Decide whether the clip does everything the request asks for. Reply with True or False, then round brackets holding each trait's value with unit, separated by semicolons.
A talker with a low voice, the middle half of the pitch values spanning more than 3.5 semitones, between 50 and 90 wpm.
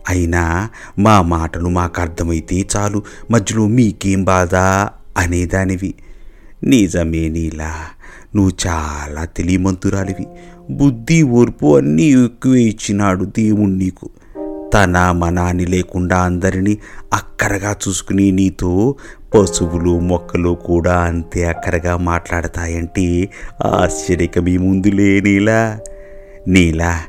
False (95 Hz; 2.7 semitones; 85 wpm)